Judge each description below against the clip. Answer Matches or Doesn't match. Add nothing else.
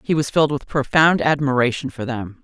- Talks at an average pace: Matches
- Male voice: Doesn't match